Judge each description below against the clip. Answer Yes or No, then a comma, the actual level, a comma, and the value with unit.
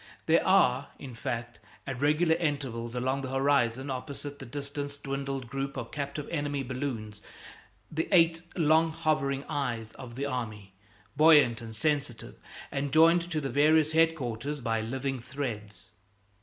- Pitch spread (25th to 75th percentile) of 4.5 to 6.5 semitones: No, average, 3.5 semitones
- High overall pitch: No, medium, 140 Hz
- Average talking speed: Yes, average, 145 wpm